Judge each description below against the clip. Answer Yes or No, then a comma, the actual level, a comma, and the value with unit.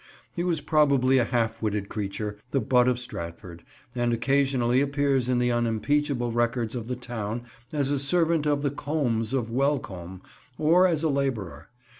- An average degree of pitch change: Yes, average, 3.8 semitones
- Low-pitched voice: Yes, low, 125 Hz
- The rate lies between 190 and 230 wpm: No, average, 165 wpm